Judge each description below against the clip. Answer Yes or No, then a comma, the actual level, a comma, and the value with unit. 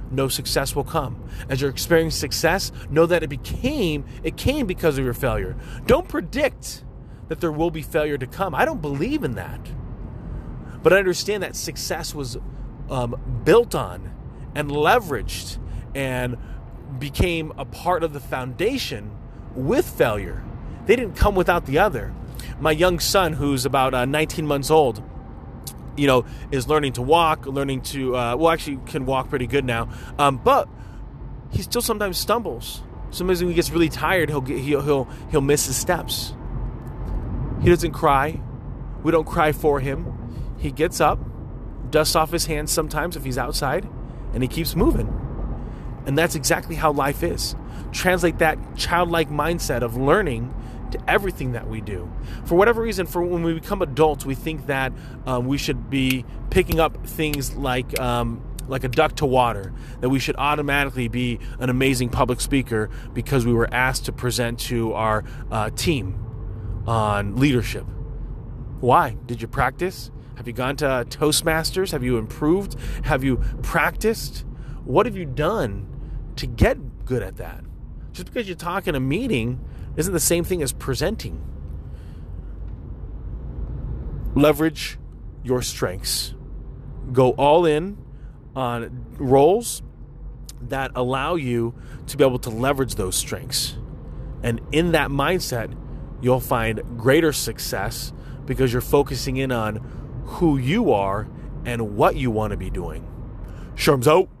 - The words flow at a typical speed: Yes, average, 155 wpm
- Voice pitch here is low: Yes, low, 130 Hz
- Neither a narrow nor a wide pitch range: Yes, average, 4.2 semitones